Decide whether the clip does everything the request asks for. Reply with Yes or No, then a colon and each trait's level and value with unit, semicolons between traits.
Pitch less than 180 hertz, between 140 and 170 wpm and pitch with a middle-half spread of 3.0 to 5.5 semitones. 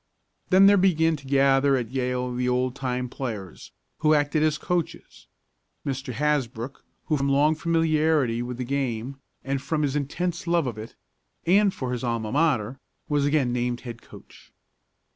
Yes: low, 135 Hz; average, 160 wpm; average, 3.7 semitones